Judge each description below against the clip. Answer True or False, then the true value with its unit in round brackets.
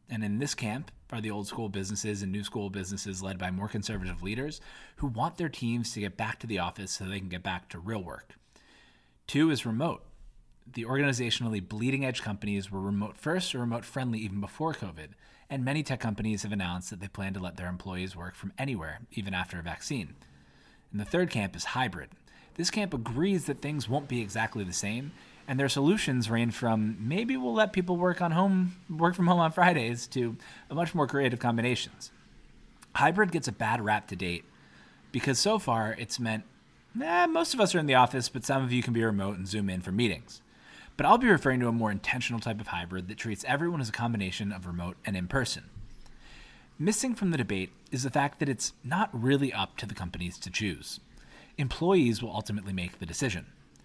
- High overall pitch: False (115 Hz)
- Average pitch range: False (6.0 semitones)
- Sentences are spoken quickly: True (210 wpm)